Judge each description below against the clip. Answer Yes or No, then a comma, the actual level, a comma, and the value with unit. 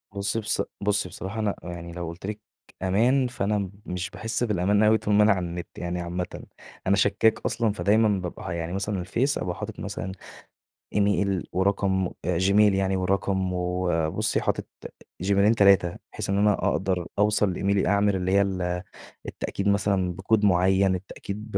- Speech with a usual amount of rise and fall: No, narrow, 2.2 semitones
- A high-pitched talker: No, low, 100 Hz